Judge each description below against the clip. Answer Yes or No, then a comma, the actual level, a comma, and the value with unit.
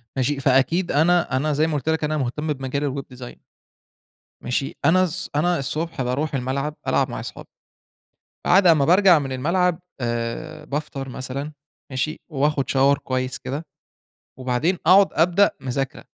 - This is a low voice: No, medium, 145 Hz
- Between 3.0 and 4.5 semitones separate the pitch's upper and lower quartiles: Yes, average, 3.6 semitones